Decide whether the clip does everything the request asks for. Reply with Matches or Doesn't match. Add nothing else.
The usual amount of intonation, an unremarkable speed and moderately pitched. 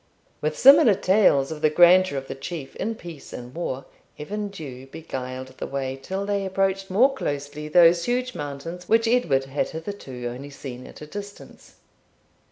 Doesn't match